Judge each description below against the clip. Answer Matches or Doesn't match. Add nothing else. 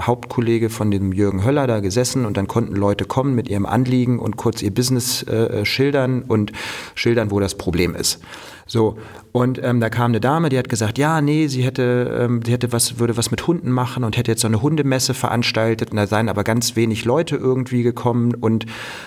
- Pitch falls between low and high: Doesn't match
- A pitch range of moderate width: Doesn't match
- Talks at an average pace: Doesn't match